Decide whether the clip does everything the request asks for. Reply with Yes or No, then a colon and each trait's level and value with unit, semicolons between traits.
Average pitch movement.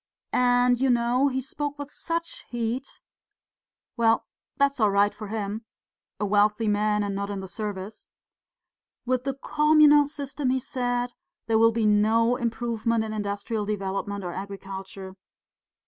Yes: average, 3.7 semitones